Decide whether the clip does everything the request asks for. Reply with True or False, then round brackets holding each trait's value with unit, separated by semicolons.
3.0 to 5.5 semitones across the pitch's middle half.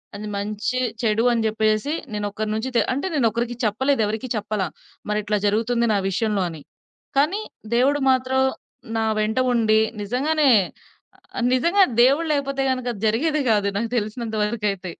True (3.7 semitones)